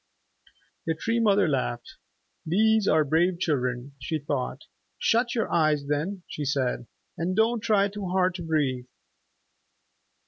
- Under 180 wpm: Yes, slow, 135 wpm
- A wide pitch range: Yes, wide, 6.1 semitones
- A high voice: No, medium, 165 Hz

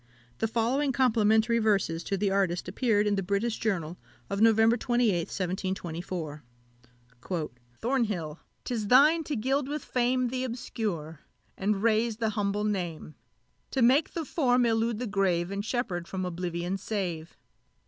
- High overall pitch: Yes, high, 210 Hz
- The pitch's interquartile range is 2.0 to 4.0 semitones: No, average, 4.6 semitones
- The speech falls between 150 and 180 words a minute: No, average, 140 wpm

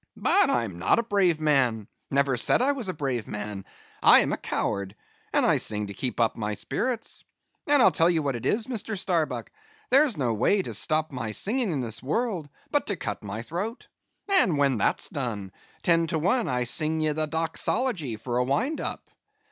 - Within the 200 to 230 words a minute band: Yes, fast, 205 wpm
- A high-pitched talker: No, medium, 150 Hz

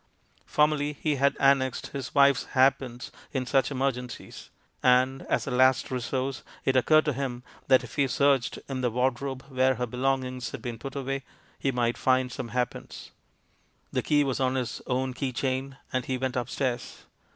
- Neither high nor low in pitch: No, low, 130 Hz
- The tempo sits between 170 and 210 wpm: Yes, average, 175 wpm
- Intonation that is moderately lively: No, narrow, 1.5 semitones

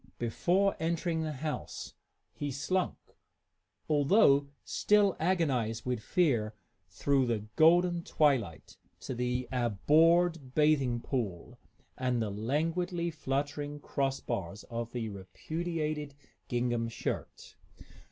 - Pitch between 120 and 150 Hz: Yes, medium, 140 Hz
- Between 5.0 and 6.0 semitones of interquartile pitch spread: Yes, wide, 5.4 semitones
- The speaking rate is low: Yes, slow, 105 wpm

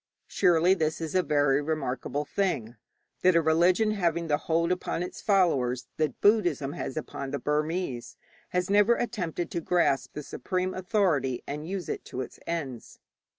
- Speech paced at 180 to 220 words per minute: No, average, 160 wpm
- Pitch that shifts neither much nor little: Yes, average, 4.1 semitones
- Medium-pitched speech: Yes, medium, 165 Hz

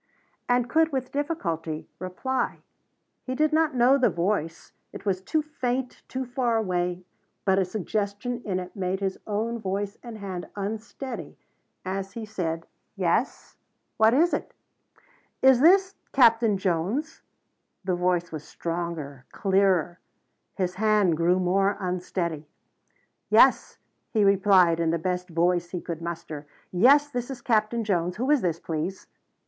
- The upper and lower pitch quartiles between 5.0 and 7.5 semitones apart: Yes, wide, 5.5 semitones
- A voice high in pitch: Yes, high, 195 Hz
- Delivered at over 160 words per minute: No, average, 140 wpm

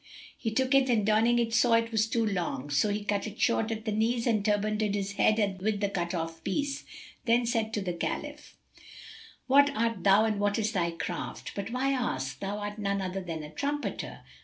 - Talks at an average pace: No, fast, 210 wpm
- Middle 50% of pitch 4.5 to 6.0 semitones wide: No, average, 2.7 semitones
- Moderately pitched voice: No, high, 215 Hz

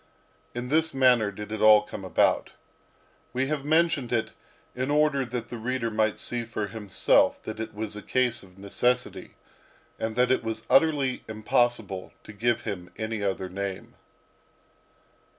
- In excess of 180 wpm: No, average, 155 wpm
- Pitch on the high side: No, low, 115 Hz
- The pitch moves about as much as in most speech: Yes, average, 3.4 semitones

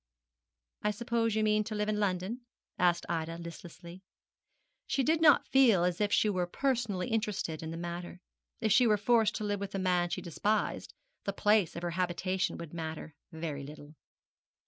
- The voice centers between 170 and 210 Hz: Yes, high, 190 Hz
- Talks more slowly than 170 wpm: No, average, 180 wpm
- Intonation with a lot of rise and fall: No, average, 3.9 semitones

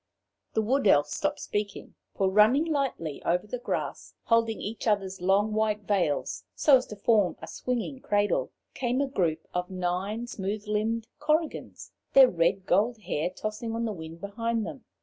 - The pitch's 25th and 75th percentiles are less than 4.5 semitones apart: Yes, average, 3.7 semitones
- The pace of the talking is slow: No, average, 170 wpm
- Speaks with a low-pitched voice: No, high, 210 Hz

